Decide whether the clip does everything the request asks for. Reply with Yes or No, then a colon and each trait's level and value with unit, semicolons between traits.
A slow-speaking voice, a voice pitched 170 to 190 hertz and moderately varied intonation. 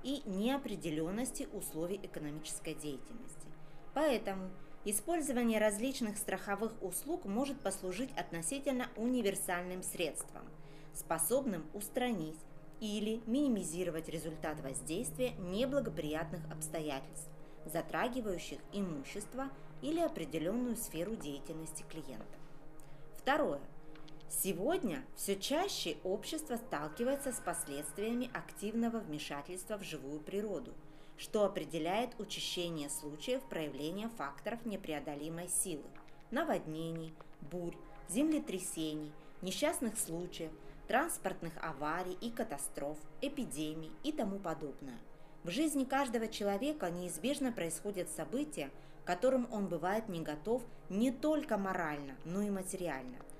No: slow, 95 wpm; medium, 185 Hz; wide, 6.8 semitones